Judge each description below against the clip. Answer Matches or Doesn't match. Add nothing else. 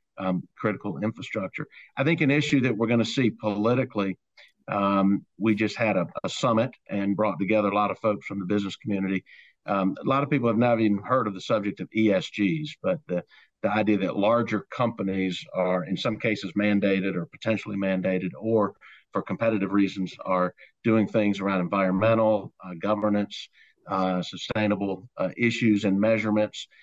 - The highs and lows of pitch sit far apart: Doesn't match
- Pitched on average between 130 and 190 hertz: Doesn't match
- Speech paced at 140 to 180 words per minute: Matches